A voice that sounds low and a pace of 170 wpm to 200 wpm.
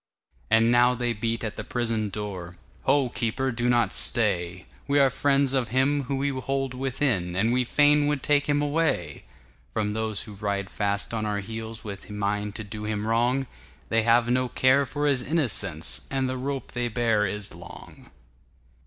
No: low, 115 Hz; average, 160 wpm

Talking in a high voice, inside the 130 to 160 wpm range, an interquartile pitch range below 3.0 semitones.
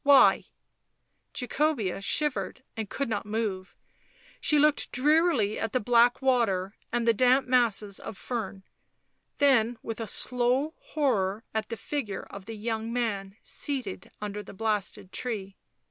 No: high, 230 Hz; average, 145 wpm; average, 3.9 semitones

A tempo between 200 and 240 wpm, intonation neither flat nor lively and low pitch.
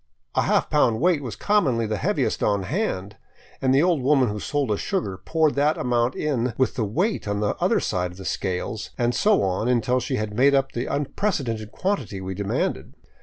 No: fast, 205 wpm; wide, 5.7 semitones; low, 125 Hz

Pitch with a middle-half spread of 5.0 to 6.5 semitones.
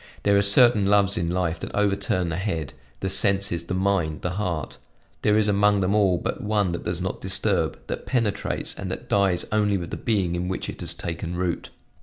No: average, 2.7 semitones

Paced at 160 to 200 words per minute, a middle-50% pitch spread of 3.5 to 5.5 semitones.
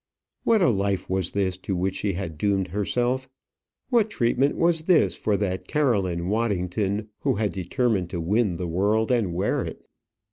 Yes: average, 170 wpm; average, 4.5 semitones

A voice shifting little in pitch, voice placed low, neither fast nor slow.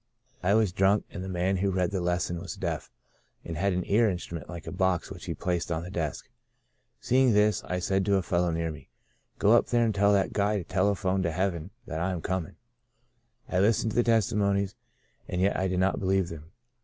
No: narrow, 2.3 semitones; very low, 95 Hz; fast, 225 wpm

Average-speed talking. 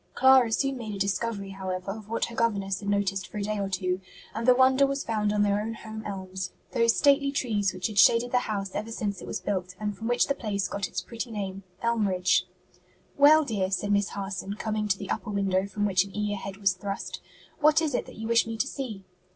No: fast, 235 wpm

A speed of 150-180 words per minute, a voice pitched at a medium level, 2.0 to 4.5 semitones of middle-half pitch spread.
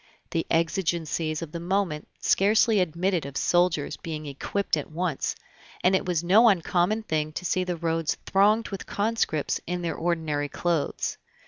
Yes: average, 155 wpm; medium, 175 Hz; average, 3.3 semitones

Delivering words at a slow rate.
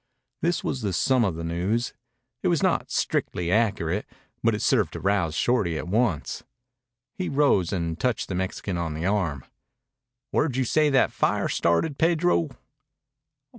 No: average, 160 wpm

